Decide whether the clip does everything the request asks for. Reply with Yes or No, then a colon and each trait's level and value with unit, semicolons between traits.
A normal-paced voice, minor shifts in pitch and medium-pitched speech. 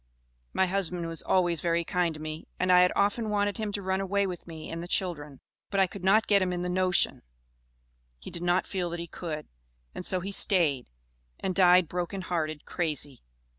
No: fast, 210 wpm; narrow, 2.3 semitones; medium, 180 Hz